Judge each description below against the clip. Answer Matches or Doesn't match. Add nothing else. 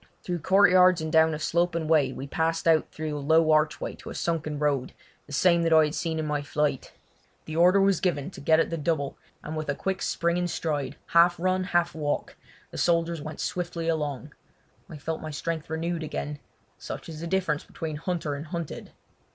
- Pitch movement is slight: Matches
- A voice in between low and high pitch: Matches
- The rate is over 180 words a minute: Matches